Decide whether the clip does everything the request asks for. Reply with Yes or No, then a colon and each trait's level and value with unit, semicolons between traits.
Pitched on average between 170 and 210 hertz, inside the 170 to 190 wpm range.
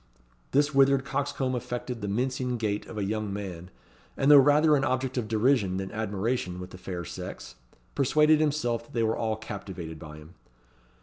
No: low, 115 Hz; average, 175 wpm